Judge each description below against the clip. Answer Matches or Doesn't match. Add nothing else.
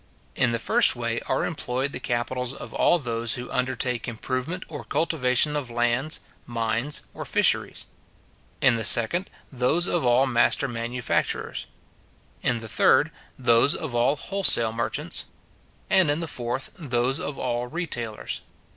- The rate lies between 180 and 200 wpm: Doesn't match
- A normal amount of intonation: Matches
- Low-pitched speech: Matches